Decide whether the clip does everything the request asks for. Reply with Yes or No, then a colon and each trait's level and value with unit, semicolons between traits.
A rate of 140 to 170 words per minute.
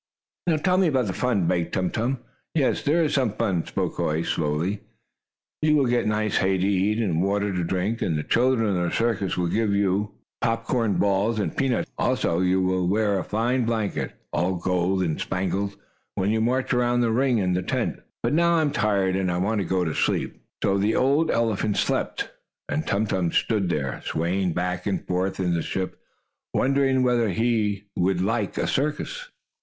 No: average, 200 wpm